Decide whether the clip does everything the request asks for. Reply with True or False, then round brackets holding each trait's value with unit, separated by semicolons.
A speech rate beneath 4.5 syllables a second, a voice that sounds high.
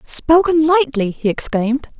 True (4.3 syllables/s; 280 Hz)